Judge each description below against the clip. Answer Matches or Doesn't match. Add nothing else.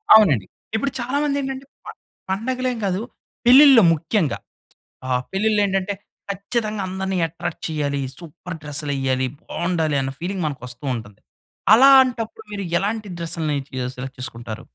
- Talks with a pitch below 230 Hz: Matches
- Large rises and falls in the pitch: Matches